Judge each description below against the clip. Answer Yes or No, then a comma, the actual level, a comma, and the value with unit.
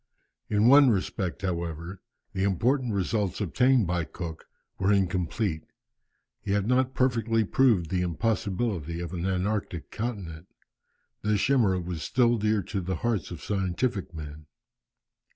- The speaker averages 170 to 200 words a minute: No, slow, 135 wpm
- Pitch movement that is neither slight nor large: Yes, average, 4.5 semitones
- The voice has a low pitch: Yes, low, 100 Hz